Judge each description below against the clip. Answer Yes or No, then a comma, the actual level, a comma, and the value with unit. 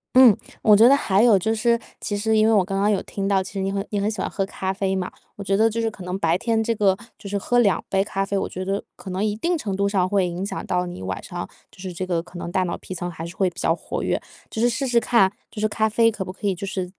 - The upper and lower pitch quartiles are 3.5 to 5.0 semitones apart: No, average, 2.7 semitones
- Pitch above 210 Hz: No, high, 195 Hz